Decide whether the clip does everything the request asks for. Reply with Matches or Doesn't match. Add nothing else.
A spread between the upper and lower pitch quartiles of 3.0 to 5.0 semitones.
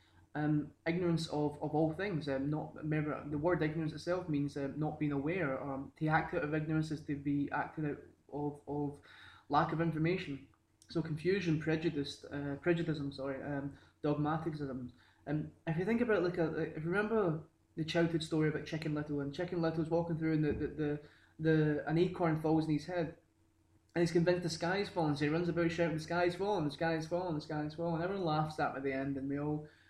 Doesn't match